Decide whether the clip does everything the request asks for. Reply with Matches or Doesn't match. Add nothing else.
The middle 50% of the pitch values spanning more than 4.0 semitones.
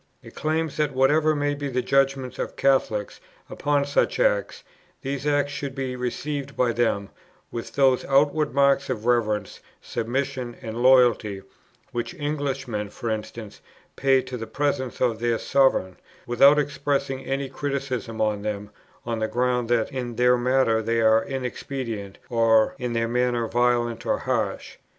Doesn't match